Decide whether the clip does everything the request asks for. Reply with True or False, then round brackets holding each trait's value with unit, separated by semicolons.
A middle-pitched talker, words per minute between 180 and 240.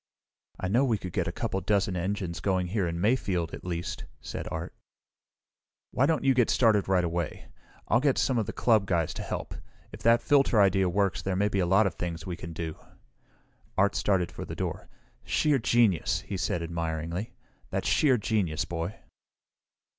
False (95 Hz; 185 wpm)